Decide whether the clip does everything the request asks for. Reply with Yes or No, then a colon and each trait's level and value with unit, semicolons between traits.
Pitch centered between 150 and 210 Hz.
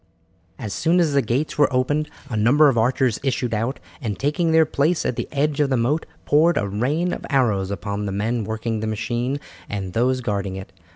No: low, 125 Hz